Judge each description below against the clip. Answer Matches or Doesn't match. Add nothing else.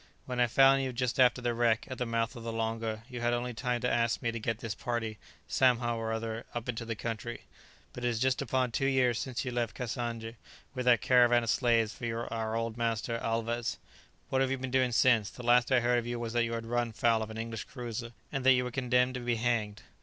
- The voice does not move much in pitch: Matches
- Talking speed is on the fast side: Matches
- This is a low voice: Matches